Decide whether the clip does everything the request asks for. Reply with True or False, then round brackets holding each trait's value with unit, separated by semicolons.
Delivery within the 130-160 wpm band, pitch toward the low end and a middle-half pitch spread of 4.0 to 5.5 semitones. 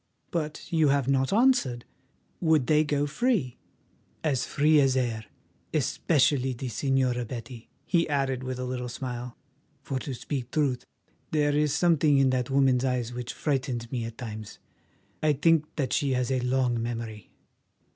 False (155 wpm; 130 Hz; 3.1 semitones)